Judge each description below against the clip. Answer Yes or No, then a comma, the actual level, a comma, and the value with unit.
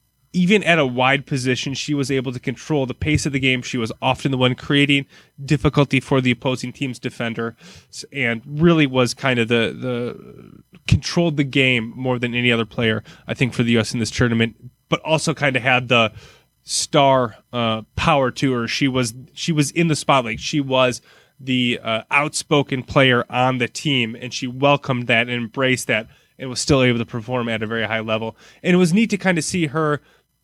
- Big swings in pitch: No, average, 3.0 semitones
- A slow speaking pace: No, fast, 205 wpm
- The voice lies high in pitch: No, low, 130 Hz